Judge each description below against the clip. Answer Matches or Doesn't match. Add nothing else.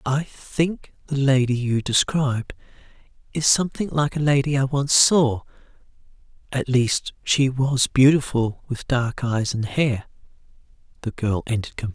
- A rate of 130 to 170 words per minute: Matches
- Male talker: Matches